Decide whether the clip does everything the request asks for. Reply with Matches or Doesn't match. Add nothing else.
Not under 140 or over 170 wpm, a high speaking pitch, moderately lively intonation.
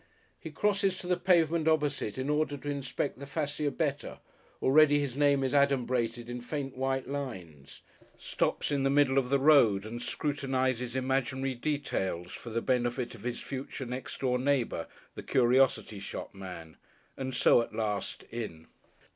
Doesn't match